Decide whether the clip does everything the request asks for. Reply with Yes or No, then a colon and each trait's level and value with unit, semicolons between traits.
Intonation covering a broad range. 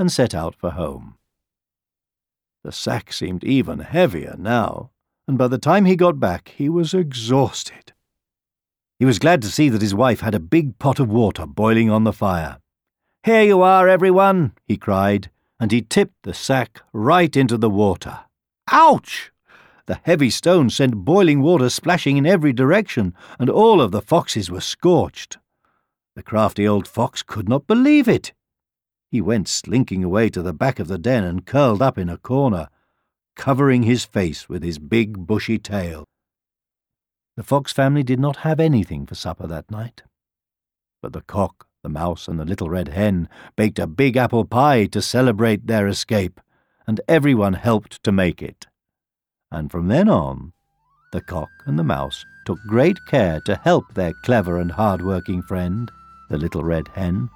Yes: wide, 6.7 semitones